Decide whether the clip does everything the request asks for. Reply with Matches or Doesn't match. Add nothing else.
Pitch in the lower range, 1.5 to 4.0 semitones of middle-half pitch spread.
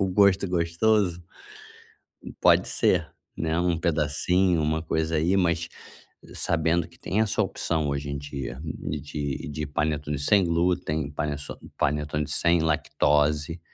Matches